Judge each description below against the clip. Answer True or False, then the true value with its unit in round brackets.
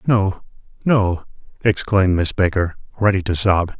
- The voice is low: True (95 Hz)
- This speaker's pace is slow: True (125 wpm)